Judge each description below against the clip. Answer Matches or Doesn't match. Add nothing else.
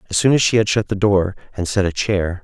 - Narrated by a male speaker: Matches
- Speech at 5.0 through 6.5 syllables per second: Matches